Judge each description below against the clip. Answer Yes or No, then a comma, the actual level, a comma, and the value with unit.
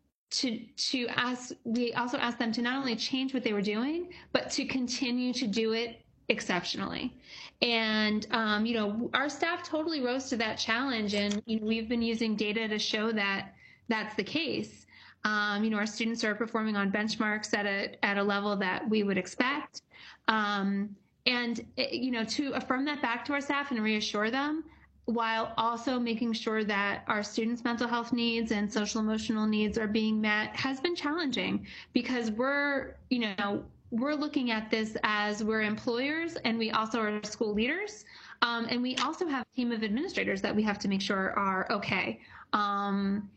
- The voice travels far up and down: No, average, 3.1 semitones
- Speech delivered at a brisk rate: No, average, 185 wpm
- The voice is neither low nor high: No, high, 230 Hz